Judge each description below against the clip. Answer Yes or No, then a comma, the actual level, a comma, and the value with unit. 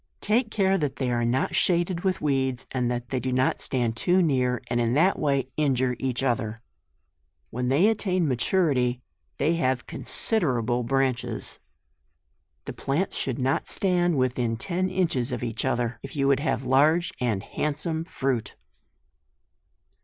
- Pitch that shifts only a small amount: No, average, 5.2 semitones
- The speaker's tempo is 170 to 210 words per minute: No, average, 155 wpm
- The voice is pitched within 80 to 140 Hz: Yes, low, 135 Hz